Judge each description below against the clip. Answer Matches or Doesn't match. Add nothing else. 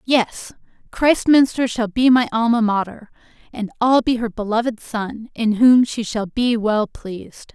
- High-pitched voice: Matches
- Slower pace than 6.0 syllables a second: Matches